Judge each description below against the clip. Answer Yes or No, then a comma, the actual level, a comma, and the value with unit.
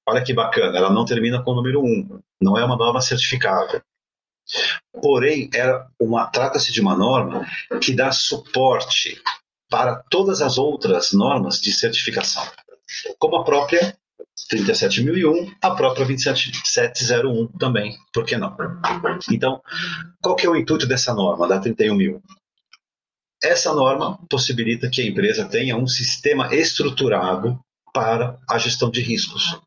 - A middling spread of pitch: No, wide, 8.0 semitones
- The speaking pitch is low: Yes, low, 130 Hz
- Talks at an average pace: Yes, average, 140 wpm